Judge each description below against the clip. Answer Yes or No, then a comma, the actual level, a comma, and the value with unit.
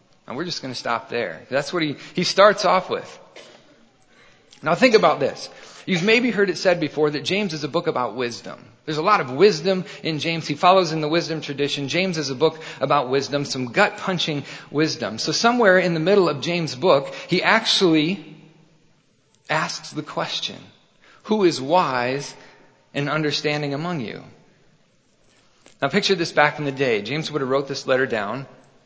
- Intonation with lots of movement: No, average, 4.2 semitones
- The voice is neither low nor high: Yes, medium, 155 Hz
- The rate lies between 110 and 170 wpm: No, average, 185 wpm